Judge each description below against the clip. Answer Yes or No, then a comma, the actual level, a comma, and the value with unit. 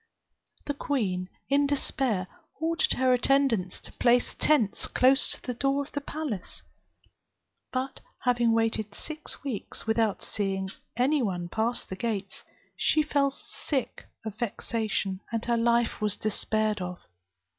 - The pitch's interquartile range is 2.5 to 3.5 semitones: No, average, 4.7 semitones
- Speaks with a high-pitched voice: Yes, high, 235 Hz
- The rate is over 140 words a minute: No, slow, 135 wpm